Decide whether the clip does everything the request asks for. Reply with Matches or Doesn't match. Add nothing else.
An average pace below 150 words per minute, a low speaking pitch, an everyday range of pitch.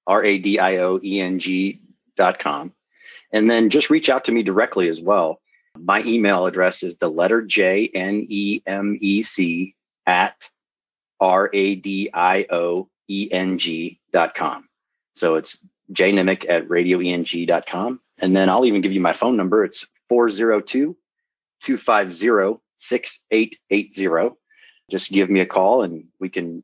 Matches